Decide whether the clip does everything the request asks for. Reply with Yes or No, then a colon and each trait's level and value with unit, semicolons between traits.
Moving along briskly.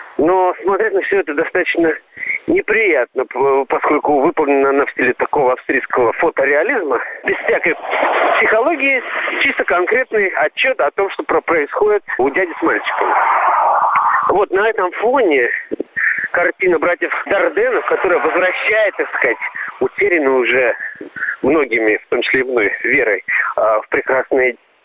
No: average, 125 wpm